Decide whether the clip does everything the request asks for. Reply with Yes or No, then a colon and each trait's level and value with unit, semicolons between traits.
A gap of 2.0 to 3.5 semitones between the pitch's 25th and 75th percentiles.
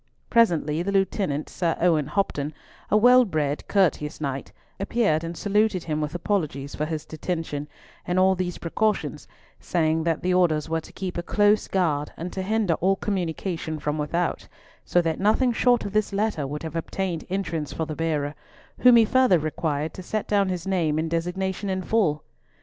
No: average, 4.1 semitones